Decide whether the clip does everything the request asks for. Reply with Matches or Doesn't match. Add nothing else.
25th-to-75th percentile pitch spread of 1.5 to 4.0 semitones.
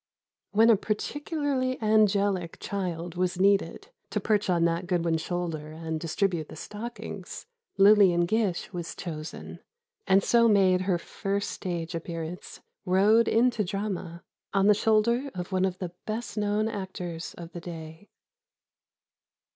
Matches